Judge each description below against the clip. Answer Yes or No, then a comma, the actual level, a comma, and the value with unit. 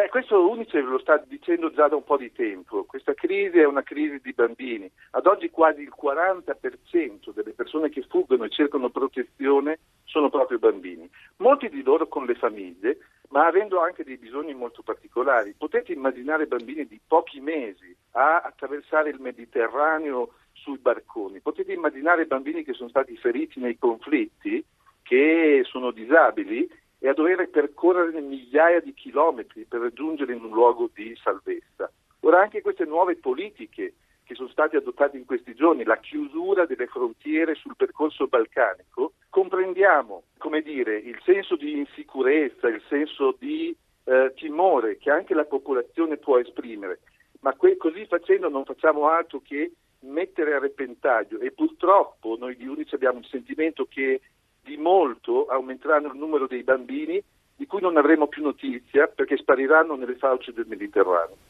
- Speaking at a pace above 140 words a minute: Yes, average, 155 wpm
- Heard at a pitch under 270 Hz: No, very high, 300 Hz